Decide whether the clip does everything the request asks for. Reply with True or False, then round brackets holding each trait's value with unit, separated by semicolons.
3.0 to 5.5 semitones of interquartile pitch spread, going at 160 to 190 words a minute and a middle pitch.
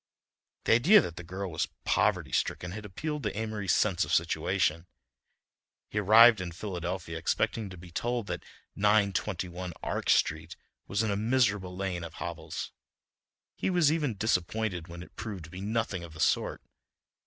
False (4.0 semitones; 165 wpm; 100 Hz)